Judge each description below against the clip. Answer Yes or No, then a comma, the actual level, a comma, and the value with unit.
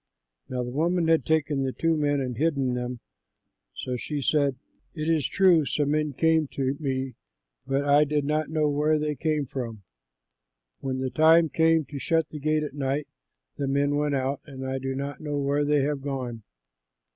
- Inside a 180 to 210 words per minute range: Yes, average, 190 wpm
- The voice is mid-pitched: Yes, medium, 145 Hz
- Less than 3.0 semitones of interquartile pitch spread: Yes, narrow, 2.4 semitones